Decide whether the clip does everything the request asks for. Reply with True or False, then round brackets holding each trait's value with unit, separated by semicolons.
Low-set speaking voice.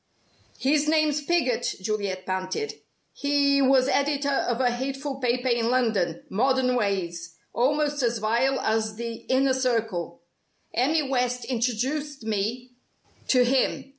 False (250 Hz)